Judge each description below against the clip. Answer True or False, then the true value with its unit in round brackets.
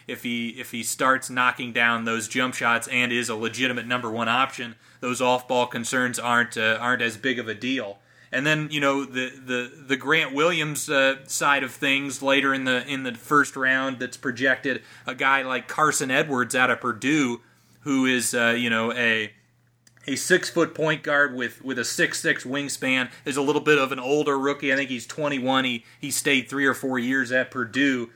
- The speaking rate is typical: False (210 wpm)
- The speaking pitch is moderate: False (130 Hz)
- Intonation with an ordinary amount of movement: False (2.1 semitones)